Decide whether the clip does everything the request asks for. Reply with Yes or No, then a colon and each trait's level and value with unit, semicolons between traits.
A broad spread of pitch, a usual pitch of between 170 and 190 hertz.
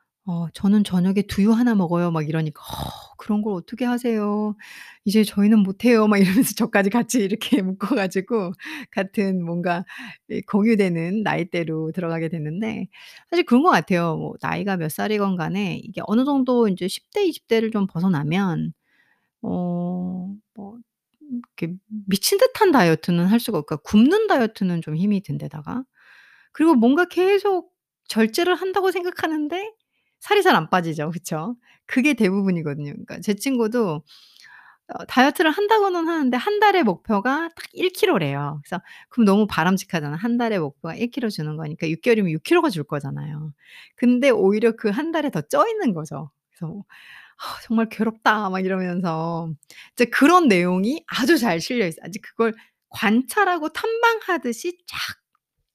No: wide, 6.4 semitones; high, 210 Hz